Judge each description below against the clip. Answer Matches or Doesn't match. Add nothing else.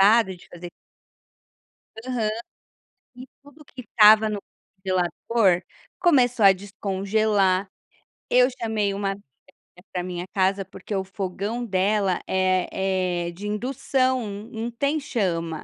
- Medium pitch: Doesn't match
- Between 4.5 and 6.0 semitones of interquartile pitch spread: Doesn't match